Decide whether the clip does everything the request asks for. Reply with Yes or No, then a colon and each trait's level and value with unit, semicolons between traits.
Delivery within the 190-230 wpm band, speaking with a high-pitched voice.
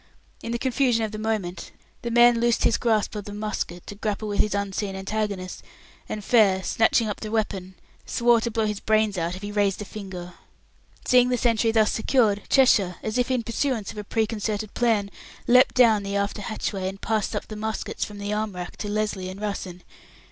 Yes: fast, 205 wpm; high, 215 Hz